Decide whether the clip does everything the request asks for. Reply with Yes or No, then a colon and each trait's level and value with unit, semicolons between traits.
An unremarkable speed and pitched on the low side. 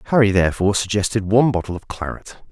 Yes: average, 165 wpm; low, 100 Hz